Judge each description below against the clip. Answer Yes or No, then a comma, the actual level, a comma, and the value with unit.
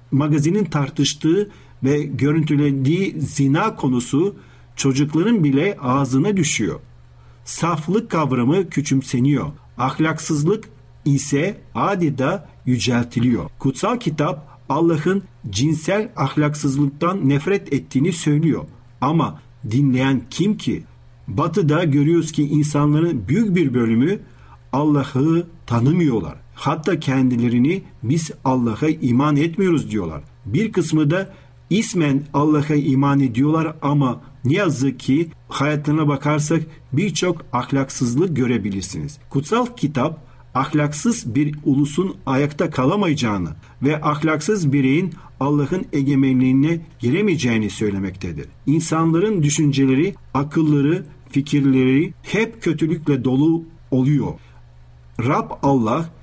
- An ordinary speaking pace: No, slow, 90 wpm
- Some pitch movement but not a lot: Yes, average, 3.6 semitones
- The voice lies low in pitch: No, medium, 145 Hz